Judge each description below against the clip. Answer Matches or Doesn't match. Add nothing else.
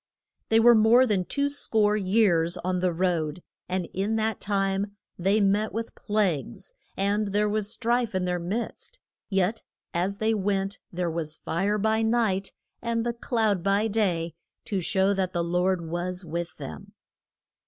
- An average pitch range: Matches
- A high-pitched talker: Matches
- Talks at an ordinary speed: Matches